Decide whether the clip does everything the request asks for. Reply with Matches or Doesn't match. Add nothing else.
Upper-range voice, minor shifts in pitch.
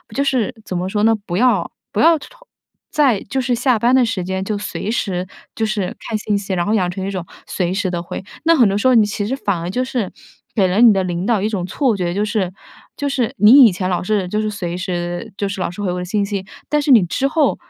Doesn't match